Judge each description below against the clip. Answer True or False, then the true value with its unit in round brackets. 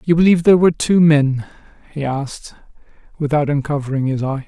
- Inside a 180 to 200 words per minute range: False (160 wpm)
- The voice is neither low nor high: True (150 Hz)